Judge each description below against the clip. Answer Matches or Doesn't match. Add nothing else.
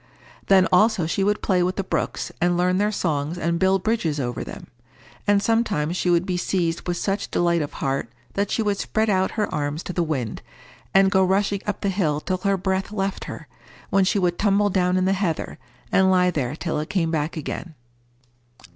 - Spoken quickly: Matches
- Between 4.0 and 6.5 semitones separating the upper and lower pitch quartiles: Doesn't match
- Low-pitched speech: Doesn't match